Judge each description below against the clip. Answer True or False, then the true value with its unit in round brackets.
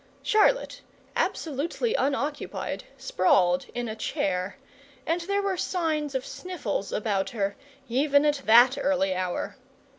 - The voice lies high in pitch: True (270 Hz)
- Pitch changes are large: True (8.0 semitones)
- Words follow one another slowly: True (120 wpm)